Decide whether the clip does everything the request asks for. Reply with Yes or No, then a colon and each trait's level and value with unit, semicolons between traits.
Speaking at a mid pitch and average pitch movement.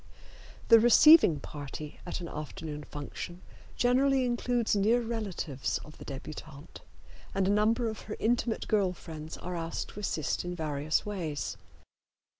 No: medium, 180 Hz; wide, 6.9 semitones